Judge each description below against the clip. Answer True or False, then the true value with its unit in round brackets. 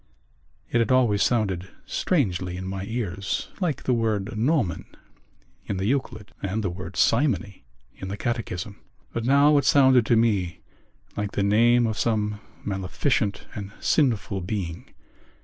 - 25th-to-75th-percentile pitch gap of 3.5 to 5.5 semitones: True (3.9 semitones)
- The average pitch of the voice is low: True (105 Hz)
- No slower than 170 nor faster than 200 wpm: False (145 wpm)